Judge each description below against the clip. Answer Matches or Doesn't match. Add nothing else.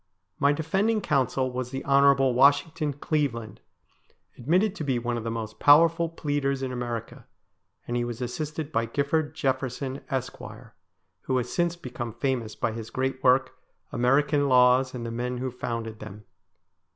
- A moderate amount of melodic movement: Matches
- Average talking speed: Matches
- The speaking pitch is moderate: Doesn't match